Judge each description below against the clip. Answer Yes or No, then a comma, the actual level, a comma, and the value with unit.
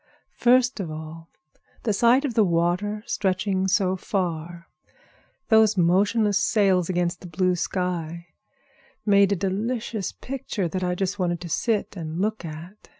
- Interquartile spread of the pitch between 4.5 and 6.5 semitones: No, average, 3.3 semitones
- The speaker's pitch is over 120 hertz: Yes, high, 190 Hz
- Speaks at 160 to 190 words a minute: No, average, 150 wpm